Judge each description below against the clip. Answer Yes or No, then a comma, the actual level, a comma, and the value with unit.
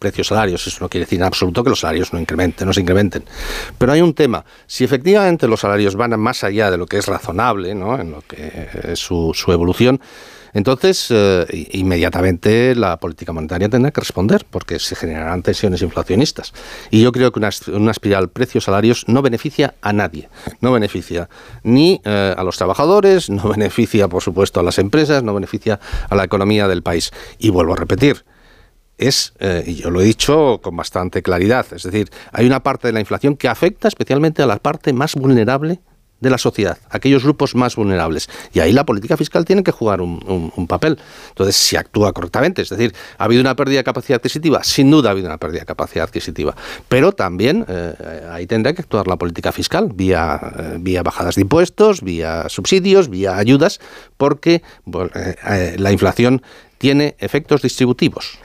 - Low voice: Yes, low, 105 Hz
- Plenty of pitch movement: Yes, wide, 6.4 semitones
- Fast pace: Yes, fast, 195 wpm